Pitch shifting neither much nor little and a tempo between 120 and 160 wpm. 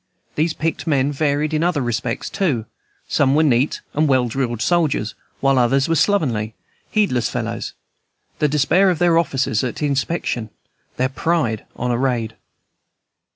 Yes: average, 4.7 semitones; average, 150 wpm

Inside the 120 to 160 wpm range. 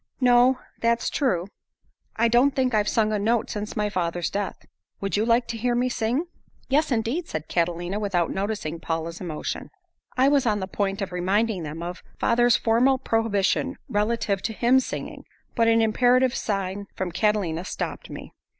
No: average, 170 wpm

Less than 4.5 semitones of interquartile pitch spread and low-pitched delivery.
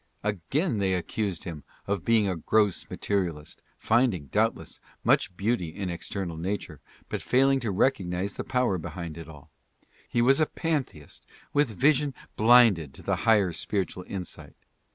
No: wide, 5.6 semitones; low, 100 Hz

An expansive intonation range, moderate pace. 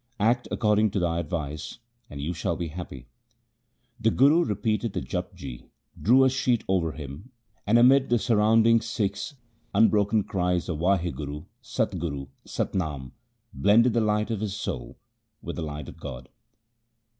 Yes: wide, 5.7 semitones; average, 155 wpm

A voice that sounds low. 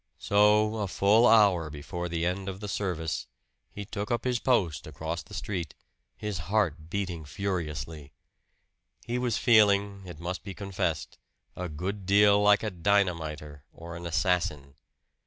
Yes: very low, 95 Hz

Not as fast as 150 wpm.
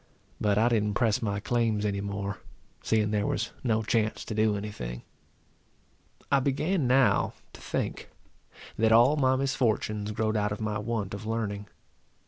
No: average, 160 wpm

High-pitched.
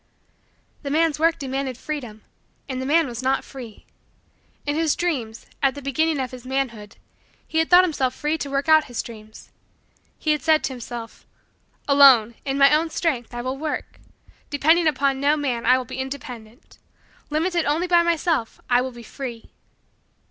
Yes: very high, 275 Hz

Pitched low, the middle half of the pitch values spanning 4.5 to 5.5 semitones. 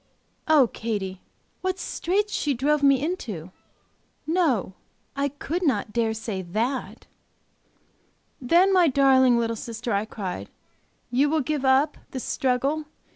No: very high, 265 Hz; average, 5.1 semitones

